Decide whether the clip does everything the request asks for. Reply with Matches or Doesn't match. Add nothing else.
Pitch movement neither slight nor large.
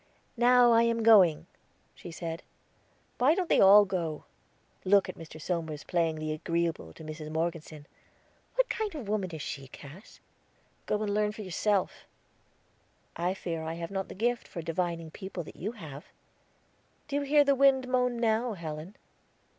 Doesn't match